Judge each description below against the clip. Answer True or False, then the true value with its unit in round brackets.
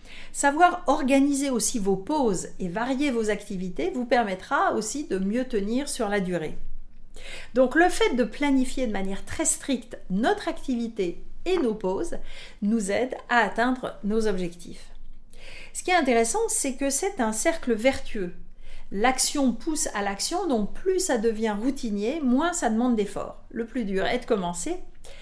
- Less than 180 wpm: True (160 wpm)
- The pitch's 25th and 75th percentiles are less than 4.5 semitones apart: False (5.3 semitones)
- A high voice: True (245 Hz)